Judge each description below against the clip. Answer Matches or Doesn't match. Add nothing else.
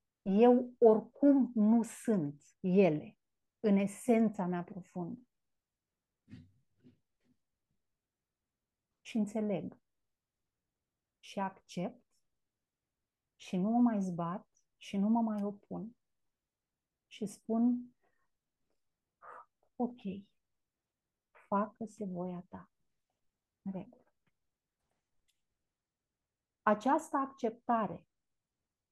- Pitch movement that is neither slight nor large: Matches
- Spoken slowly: Matches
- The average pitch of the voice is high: Matches